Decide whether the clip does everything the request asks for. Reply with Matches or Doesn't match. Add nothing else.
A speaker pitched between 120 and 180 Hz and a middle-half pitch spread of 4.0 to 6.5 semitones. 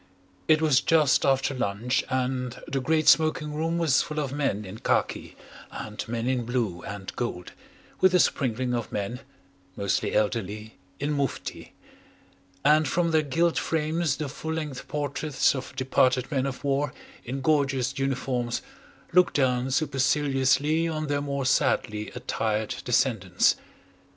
Doesn't match